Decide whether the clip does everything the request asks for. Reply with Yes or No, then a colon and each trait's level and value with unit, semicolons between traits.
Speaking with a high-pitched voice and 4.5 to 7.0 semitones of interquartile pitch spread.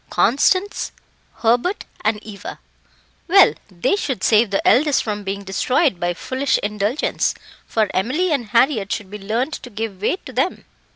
Yes: high, 225 Hz; average, 5.2 semitones